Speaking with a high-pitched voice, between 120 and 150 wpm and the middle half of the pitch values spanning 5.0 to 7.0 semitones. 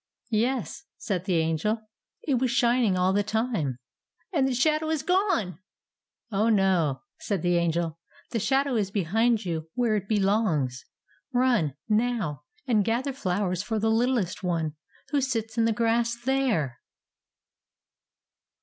Yes: high, 215 Hz; average, 140 wpm; average, 5.3 semitones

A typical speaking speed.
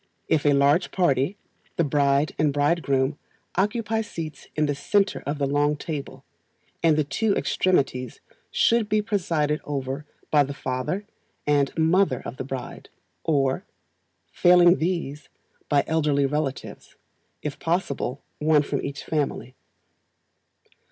No: slow, 130 wpm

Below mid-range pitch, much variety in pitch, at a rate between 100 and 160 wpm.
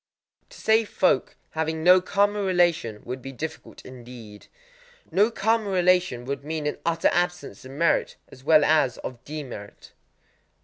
No: medium, 160 Hz; wide, 5.9 semitones; average, 150 wpm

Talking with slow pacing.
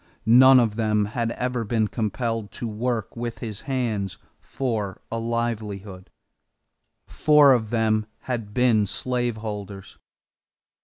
Yes: slow, 115 wpm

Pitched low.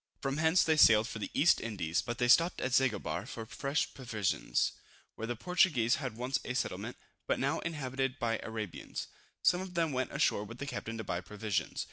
Yes: low, 125 Hz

